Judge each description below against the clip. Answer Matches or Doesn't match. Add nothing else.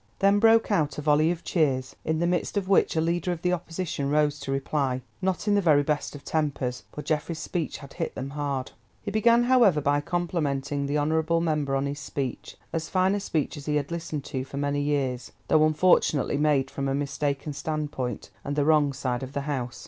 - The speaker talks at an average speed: Doesn't match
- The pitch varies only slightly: Doesn't match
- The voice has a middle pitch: Matches